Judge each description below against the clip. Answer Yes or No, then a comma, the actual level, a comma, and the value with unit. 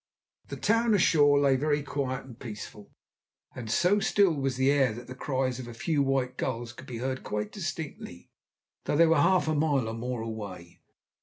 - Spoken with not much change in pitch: No, average, 4.0 semitones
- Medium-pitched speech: No, low, 130 Hz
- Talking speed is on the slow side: No, average, 190 wpm